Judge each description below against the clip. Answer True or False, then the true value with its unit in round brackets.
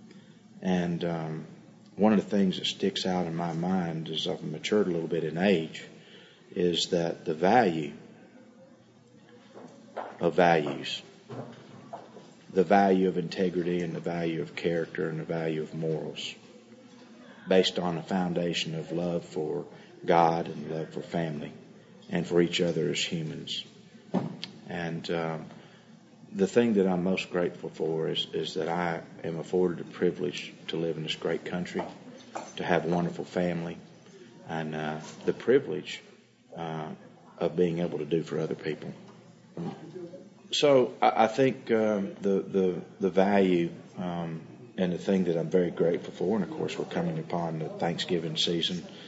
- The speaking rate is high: False (155 wpm)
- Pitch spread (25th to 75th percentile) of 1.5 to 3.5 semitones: True (3.1 semitones)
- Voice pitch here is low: True (90 Hz)